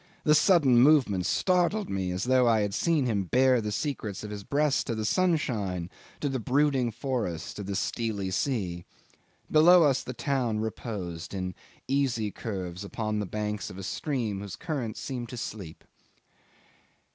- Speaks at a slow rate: No, average, 165 wpm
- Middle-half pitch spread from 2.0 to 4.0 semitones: No, wide, 5.4 semitones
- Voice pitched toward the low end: Yes, low, 115 Hz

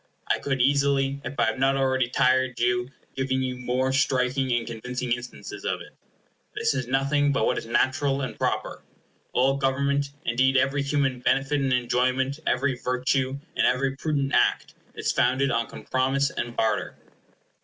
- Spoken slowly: No, average, 165 wpm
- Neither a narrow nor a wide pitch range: No, narrow, 1.6 semitones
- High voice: No, low, 130 Hz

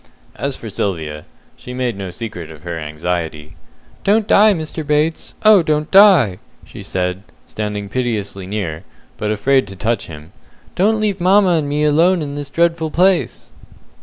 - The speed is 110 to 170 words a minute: Yes, average, 160 wpm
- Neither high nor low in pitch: No, low, 125 Hz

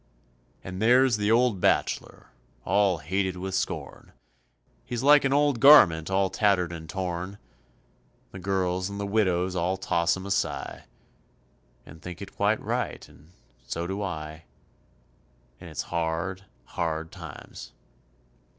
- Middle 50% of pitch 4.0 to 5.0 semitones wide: No, average, 3.0 semitones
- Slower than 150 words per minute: Yes, slow, 135 wpm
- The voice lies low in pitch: Yes, very low, 95 Hz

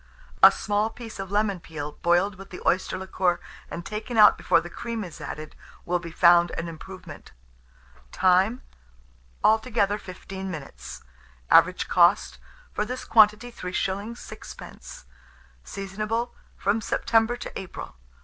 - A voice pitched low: No, high, 195 Hz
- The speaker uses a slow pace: Yes, slow, 130 wpm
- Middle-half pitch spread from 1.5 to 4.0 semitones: Yes, average, 3.6 semitones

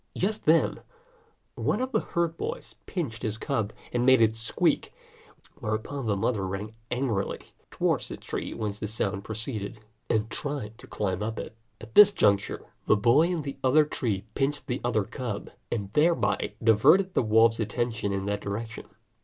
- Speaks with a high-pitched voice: No, low, 115 Hz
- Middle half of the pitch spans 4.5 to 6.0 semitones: Yes, average, 4.9 semitones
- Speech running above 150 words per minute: Yes, average, 170 wpm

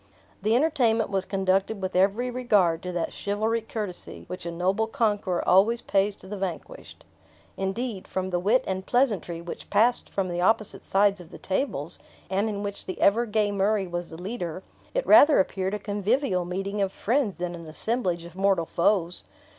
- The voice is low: No, high, 195 Hz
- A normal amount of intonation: Yes, average, 3.3 semitones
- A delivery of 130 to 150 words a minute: No, average, 180 wpm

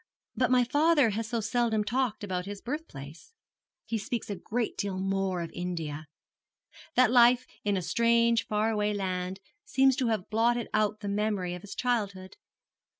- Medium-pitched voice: No, high, 215 Hz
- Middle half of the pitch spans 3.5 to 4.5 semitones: Yes, average, 3.9 semitones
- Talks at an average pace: Yes, average, 165 wpm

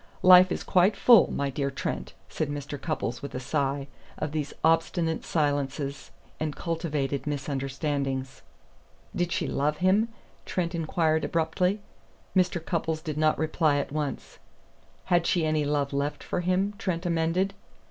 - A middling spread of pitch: Yes, average, 3.4 semitones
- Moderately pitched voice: Yes, medium, 155 Hz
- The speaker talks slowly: No, average, 145 wpm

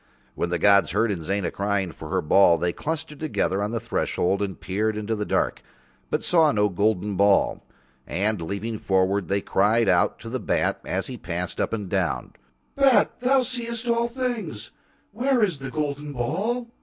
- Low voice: Yes, low, 110 Hz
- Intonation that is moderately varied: No, wide, 8.7 semitones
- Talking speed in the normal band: Yes, average, 180 wpm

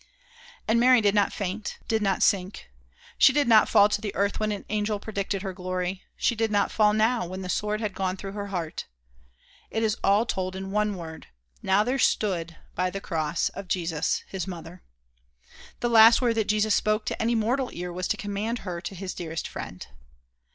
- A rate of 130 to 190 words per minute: No, average, 200 wpm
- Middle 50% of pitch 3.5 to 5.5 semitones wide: No, average, 2.8 semitones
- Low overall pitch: No, high, 200 Hz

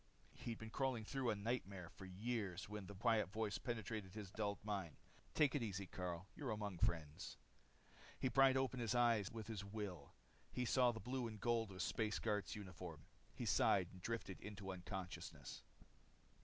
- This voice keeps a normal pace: Yes, average, 175 wpm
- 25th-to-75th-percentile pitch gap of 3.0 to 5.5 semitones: Yes, average, 3.6 semitones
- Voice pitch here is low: Yes, low, 105 Hz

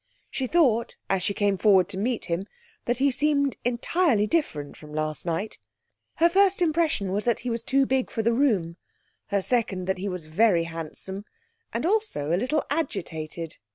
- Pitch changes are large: Yes, wide, 7.1 semitones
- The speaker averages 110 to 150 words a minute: No, average, 180 wpm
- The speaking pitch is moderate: No, high, 215 Hz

